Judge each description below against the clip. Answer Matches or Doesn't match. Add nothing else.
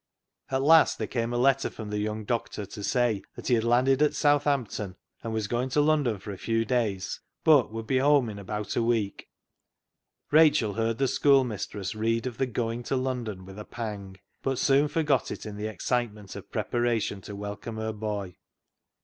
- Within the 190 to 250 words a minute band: Matches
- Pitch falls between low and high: Doesn't match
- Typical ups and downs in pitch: Matches